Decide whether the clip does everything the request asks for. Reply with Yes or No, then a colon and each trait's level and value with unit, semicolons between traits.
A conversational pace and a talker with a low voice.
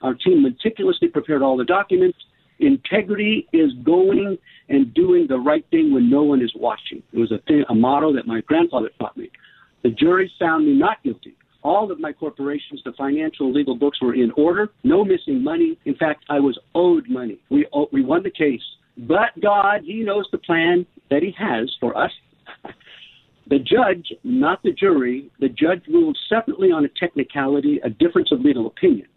No: average, 185 wpm; high, 205 Hz